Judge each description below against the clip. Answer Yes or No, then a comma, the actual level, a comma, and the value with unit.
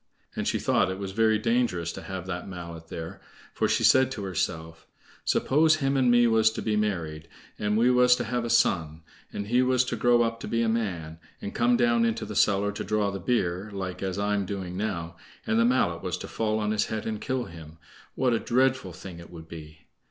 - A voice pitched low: Yes, low, 105 Hz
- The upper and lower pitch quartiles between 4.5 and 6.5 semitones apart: Yes, average, 4.9 semitones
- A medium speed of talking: No, fast, 225 wpm